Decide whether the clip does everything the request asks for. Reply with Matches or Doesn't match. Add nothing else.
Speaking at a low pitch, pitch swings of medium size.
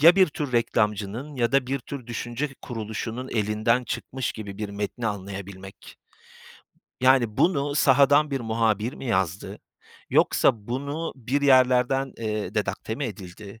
Matches